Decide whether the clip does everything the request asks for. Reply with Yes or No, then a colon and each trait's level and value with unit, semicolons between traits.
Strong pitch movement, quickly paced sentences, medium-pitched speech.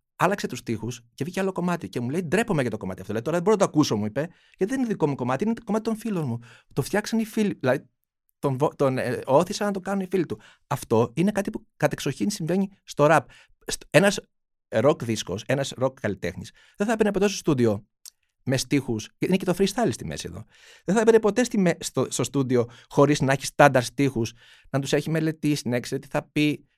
Yes: wide, 8.0 semitones; fast, 230 wpm; medium, 150 Hz